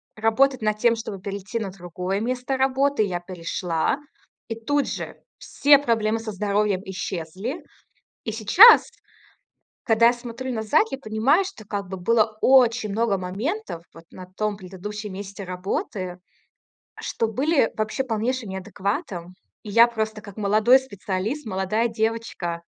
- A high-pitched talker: Yes, high, 215 Hz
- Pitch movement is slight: No, average, 3.8 semitones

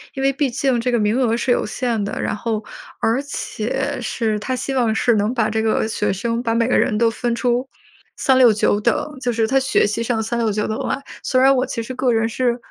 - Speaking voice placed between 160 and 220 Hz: No, high, 235 Hz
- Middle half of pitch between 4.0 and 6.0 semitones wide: No, narrow, 2.6 semitones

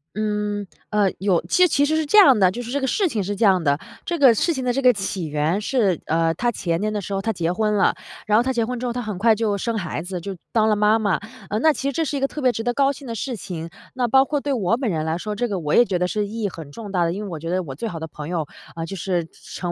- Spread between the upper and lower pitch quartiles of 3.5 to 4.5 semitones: No, average, 5.3 semitones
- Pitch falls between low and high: No, high, 210 Hz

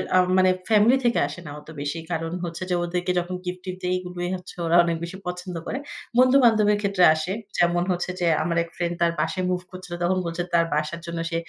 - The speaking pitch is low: No, medium, 180 Hz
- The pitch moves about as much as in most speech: No, narrow, 1.6 semitones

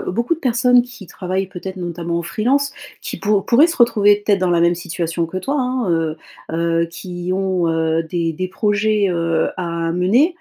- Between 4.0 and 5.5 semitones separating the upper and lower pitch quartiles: Yes, average, 4.3 semitones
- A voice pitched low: No, medium, 185 Hz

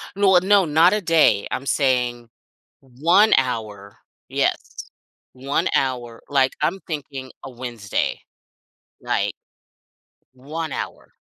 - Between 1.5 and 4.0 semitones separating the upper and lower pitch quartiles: No, average, 5.2 semitones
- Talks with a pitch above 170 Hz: No, low, 135 Hz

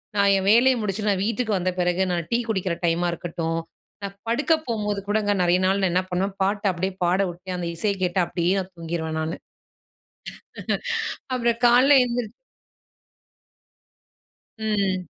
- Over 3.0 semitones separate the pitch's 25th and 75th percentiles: Yes, average, 3.4 semitones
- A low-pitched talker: No, high, 190 Hz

